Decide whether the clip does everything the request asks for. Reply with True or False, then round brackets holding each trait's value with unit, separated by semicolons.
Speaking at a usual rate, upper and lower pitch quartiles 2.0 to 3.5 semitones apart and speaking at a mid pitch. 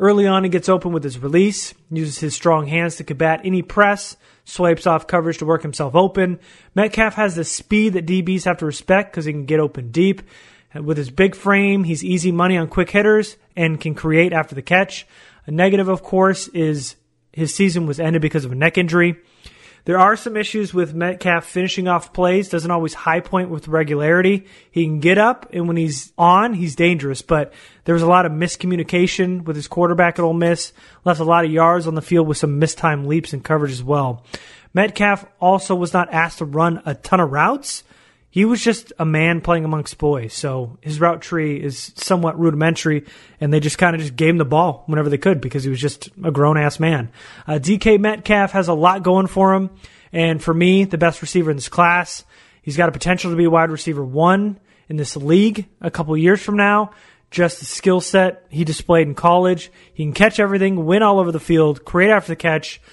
False (215 wpm; 3.0 semitones; 170 Hz)